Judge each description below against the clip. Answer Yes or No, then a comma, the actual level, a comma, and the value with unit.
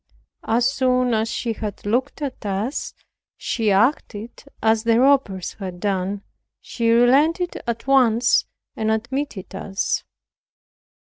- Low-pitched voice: No, high, 230 Hz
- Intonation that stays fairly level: No, average, 3.8 semitones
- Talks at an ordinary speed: No, slow, 120 wpm